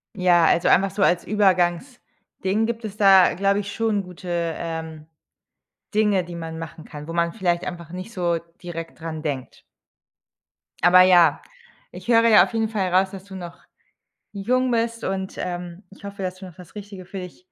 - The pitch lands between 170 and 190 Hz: Yes, medium, 185 Hz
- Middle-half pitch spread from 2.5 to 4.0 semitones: Yes, average, 2.9 semitones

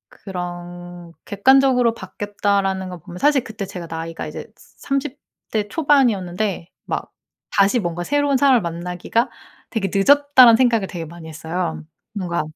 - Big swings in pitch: Yes, wide, 5.9 semitones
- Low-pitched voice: No, high, 195 Hz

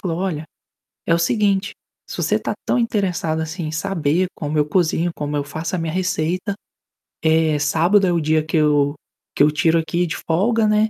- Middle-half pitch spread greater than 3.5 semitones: No, average, 3.1 semitones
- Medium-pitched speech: Yes, medium, 165 Hz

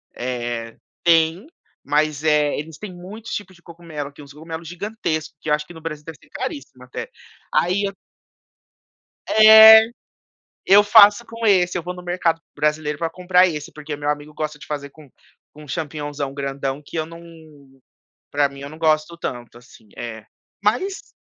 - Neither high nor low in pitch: Yes, medium, 155 Hz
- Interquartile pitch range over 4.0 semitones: No, average, 3.6 semitones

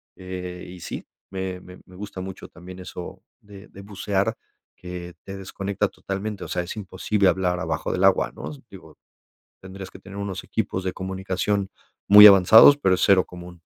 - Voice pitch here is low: Yes, very low, 95 Hz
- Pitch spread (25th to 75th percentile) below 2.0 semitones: Yes, narrow, 1.4 semitones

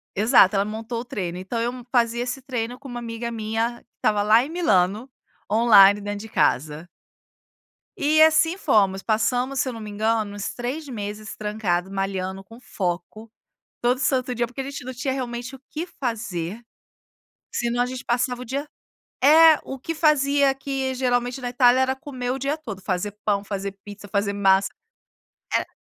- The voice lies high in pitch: Yes, high, 235 Hz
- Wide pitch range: No, average, 4.2 semitones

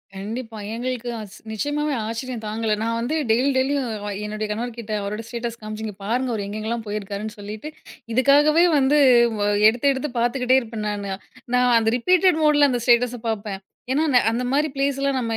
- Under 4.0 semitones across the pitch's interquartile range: Yes, average, 3.6 semitones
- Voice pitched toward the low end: No, high, 235 Hz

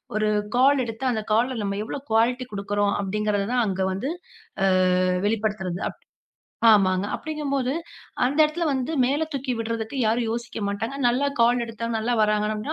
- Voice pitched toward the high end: Yes, high, 230 Hz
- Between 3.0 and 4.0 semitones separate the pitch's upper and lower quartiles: Yes, average, 3.7 semitones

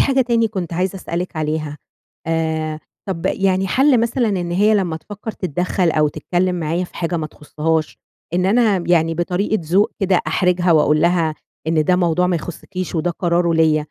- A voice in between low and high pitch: Yes, medium, 175 Hz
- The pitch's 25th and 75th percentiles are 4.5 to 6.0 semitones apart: No, average, 2.9 semitones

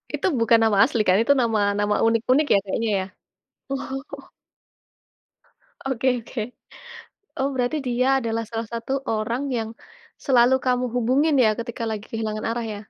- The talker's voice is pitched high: Yes, high, 235 Hz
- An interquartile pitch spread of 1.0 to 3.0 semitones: Yes, average, 2.7 semitones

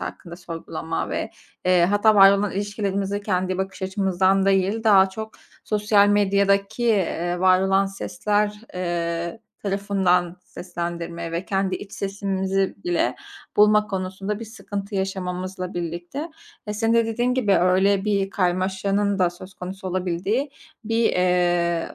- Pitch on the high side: Yes, high, 195 Hz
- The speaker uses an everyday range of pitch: No, narrow, 2.1 semitones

